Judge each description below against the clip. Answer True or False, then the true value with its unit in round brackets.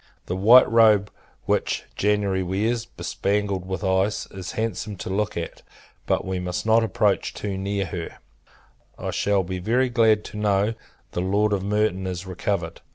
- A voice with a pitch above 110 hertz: False (100 Hz)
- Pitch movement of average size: False (2.2 semitones)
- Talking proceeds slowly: False (160 wpm)